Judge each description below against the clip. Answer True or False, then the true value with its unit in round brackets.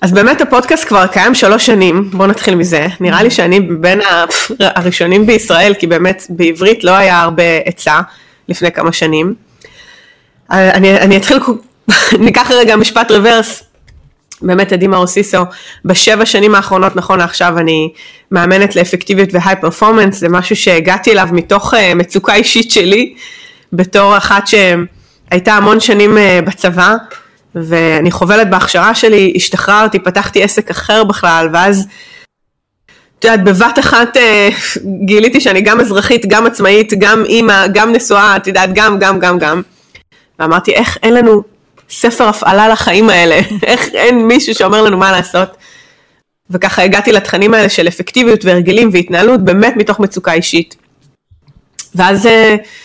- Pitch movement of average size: True (3.3 semitones)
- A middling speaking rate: True (135 wpm)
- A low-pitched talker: False (200 Hz)